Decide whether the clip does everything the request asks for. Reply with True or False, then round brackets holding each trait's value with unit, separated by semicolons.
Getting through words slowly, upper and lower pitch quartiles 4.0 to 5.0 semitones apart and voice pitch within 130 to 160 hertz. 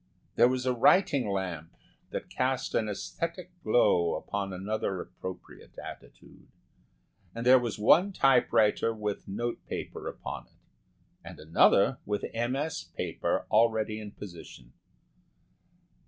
False (120 wpm; 4.3 semitones; 110 Hz)